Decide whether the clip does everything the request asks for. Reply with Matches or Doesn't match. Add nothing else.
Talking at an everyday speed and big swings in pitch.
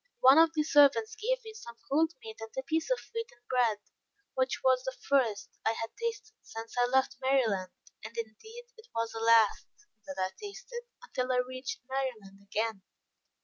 Matches